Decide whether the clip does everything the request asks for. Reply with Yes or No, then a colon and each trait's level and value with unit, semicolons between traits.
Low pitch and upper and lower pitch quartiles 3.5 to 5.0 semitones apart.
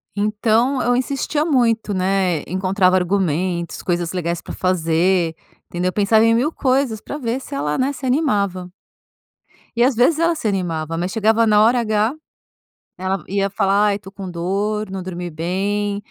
No: high, 200 Hz; average, 4.1 semitones